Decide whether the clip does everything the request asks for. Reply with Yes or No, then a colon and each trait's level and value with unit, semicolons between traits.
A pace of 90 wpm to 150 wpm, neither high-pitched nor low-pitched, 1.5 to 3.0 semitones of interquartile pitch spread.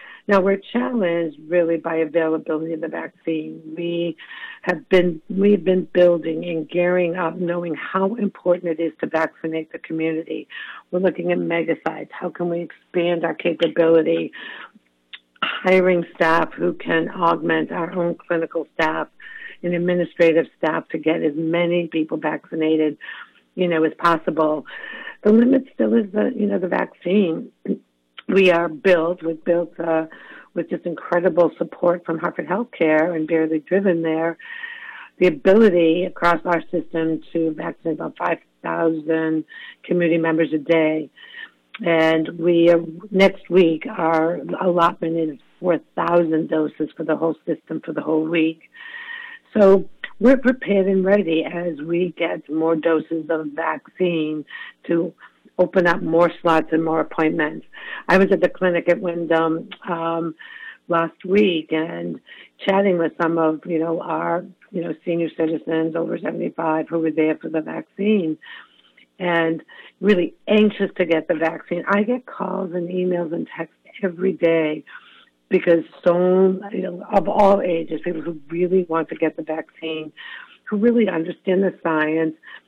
Yes: average, 145 wpm; medium, 170 Hz; narrow, 2.4 semitones